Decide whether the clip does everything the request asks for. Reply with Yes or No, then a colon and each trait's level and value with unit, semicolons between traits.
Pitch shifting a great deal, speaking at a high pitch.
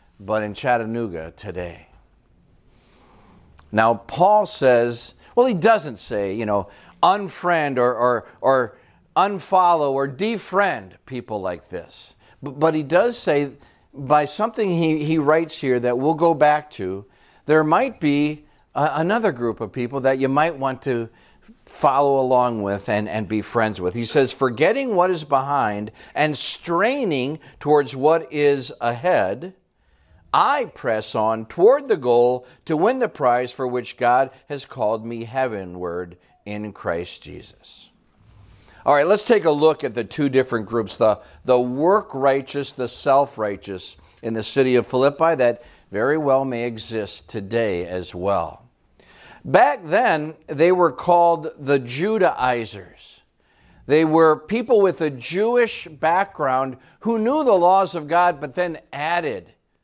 No: wide, 6.2 semitones; low, 135 Hz